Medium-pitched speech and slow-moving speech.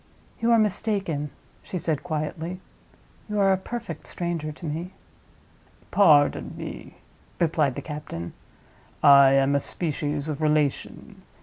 Yes: medium, 155 Hz; slow, 125 wpm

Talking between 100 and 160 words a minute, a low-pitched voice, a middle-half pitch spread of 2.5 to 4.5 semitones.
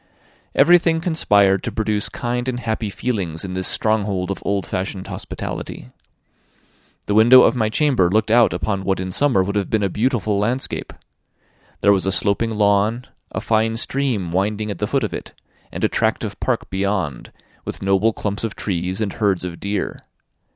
No: average, 180 wpm; low, 105 Hz; average, 3.0 semitones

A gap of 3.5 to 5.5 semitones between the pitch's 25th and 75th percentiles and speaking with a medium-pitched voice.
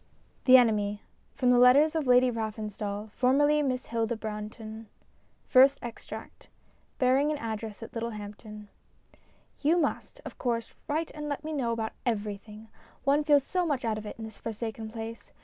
No: average, 4.0 semitones; high, 230 Hz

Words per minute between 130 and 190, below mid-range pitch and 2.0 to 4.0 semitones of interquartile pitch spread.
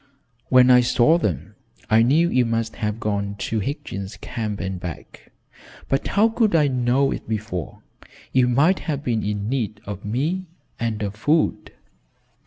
No: average, 160 wpm; low, 115 Hz; average, 4.8 semitones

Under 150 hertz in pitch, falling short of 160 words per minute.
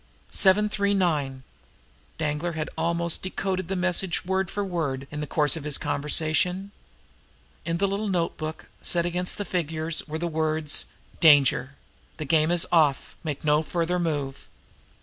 No: medium, 165 Hz; average, 150 wpm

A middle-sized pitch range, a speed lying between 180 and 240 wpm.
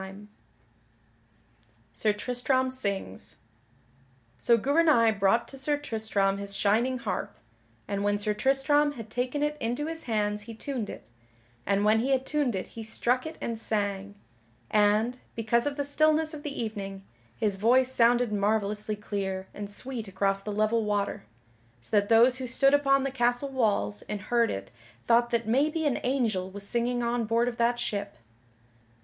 No: average, 4.0 semitones; average, 165 wpm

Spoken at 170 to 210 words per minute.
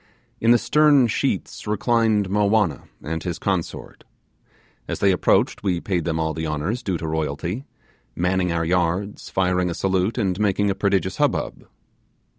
No: average, 155 wpm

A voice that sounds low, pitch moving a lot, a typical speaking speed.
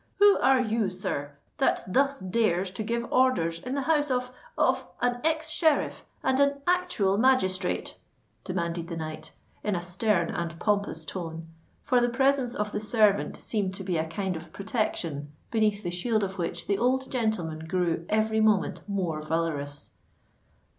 No: high, 205 Hz; wide, 6.6 semitones; average, 160 wpm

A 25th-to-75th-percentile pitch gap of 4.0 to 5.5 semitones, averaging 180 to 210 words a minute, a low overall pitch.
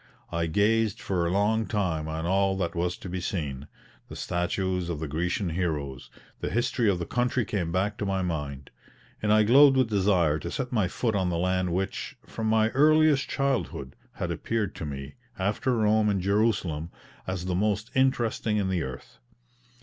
Yes: average, 4.3 semitones; average, 185 wpm; very low, 95 Hz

